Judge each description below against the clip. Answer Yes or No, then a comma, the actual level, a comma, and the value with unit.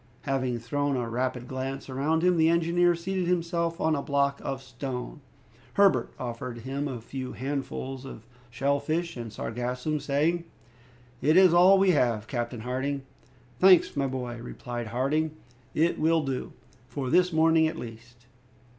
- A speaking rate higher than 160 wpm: No, average, 155 wpm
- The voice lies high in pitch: No, medium, 140 Hz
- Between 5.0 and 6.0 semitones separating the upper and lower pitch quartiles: No, average, 4.4 semitones